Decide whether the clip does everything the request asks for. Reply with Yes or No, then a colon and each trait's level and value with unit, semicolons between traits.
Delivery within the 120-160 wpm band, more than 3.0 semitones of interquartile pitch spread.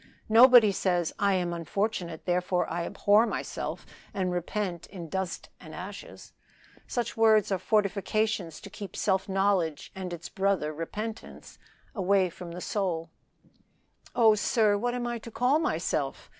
Yes: average, 140 wpm; average, 3.6 semitones